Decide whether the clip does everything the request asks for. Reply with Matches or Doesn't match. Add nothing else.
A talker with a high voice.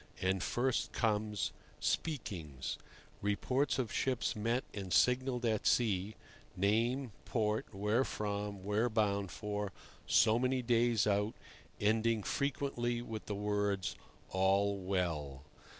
Doesn't match